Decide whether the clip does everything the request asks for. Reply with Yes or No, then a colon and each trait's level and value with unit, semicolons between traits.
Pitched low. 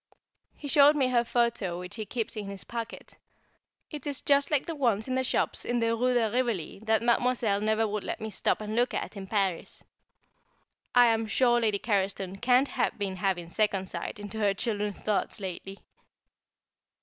No: high, 220 Hz